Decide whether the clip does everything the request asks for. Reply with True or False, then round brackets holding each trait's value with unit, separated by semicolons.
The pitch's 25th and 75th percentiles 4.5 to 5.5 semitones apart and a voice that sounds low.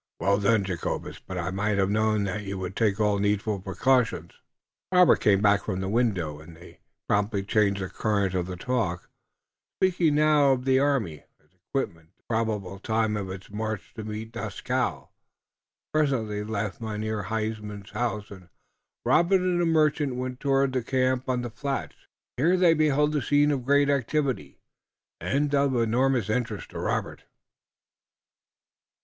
True (5.2 semitones; 110 Hz)